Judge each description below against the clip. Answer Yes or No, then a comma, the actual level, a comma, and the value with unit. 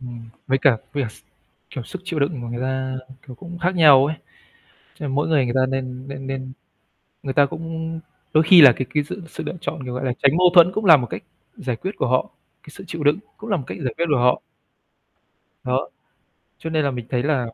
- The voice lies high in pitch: No, medium, 140 Hz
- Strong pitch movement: No, average, 4.0 semitones